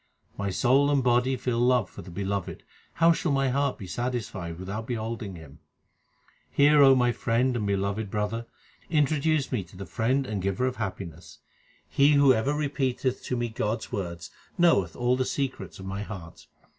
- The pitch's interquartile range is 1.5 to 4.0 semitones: No, average, 5.3 semitones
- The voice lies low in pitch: Yes, low, 120 Hz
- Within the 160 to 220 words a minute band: Yes, average, 175 wpm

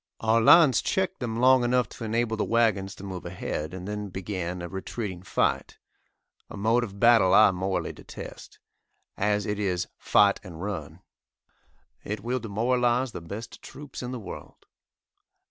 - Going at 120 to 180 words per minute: Yes, average, 160 wpm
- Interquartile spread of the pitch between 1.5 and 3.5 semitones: No, average, 3.9 semitones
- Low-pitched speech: Yes, low, 105 Hz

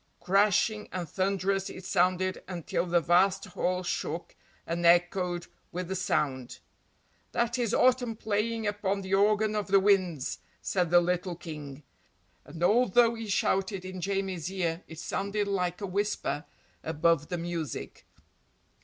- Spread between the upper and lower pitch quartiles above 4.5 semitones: No, average, 2.7 semitones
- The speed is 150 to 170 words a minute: No, average, 140 wpm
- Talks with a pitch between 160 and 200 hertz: Yes, medium, 185 Hz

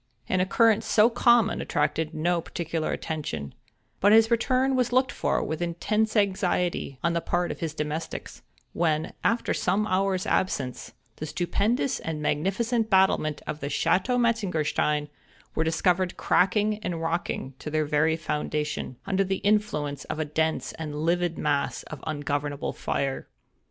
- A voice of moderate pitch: Yes, medium, 170 Hz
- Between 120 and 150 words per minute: Yes, average, 145 wpm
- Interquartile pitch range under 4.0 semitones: No, average, 5.3 semitones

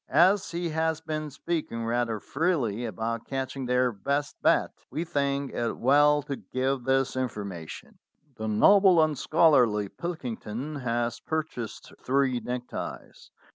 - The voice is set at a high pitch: No, low, 135 Hz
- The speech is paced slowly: Yes, slow, 130 wpm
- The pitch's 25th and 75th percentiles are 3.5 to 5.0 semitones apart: Yes, average, 4.7 semitones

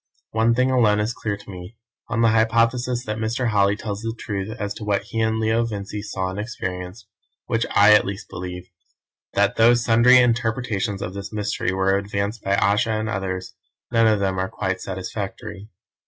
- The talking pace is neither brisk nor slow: Yes, average, 185 wpm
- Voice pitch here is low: Yes, low, 105 Hz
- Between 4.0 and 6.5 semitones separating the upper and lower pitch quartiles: No, average, 2.7 semitones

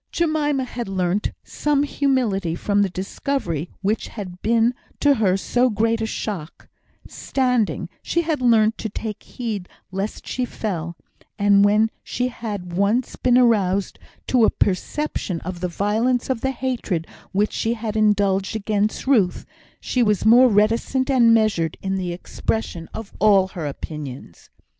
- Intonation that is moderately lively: Yes, average, 4.3 semitones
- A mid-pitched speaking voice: No, high, 215 Hz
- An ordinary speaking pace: Yes, average, 150 wpm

